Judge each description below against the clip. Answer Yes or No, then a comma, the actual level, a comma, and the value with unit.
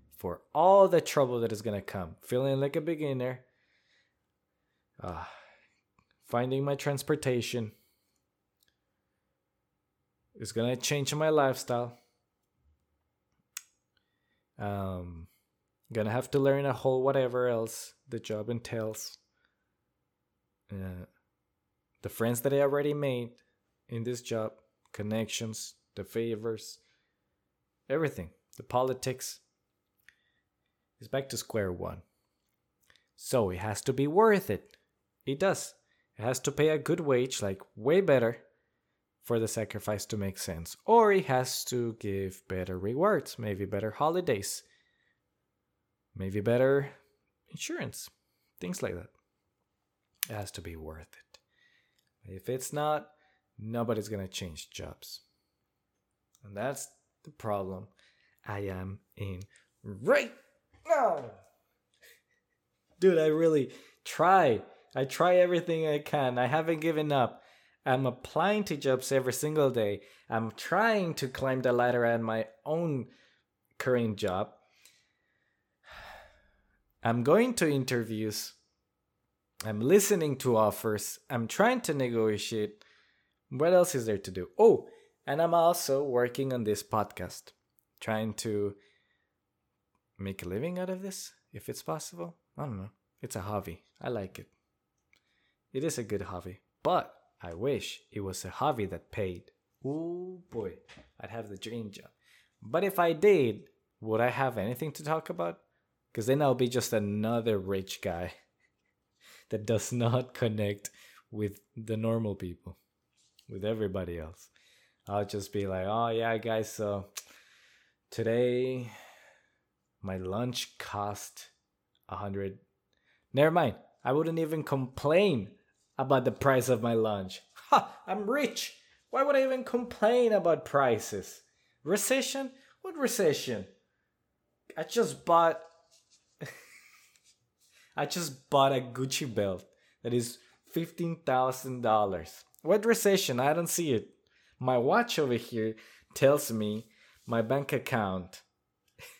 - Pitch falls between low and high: No, low, 120 Hz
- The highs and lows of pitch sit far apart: Yes, wide, 6.0 semitones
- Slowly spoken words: Yes, slow, 125 wpm